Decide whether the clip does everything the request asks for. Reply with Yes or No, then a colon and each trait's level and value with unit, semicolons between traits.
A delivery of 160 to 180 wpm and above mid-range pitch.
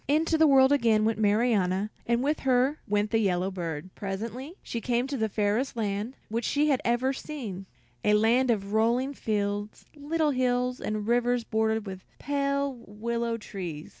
Yes: average, 165 wpm; high, 230 Hz